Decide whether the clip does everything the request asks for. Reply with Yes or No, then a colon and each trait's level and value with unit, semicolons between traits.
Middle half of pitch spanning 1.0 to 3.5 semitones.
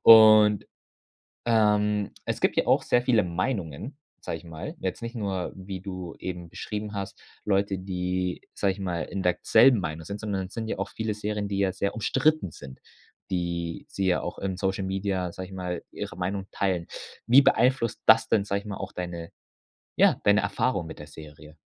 Yes: average, 2.8 semitones